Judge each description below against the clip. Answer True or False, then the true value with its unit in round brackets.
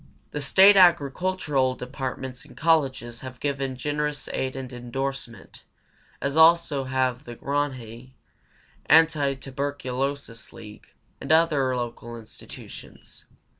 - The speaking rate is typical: False (100 wpm)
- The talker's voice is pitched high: False (135 Hz)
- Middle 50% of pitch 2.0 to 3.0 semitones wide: True (2.6 semitones)